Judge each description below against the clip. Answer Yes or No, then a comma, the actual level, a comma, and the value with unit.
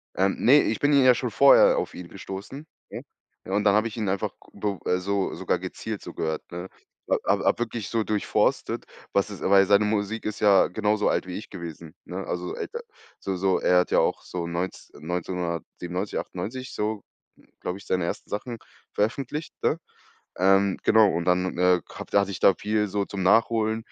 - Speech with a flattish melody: No, average, 3.2 semitones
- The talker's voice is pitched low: Yes, low, 100 Hz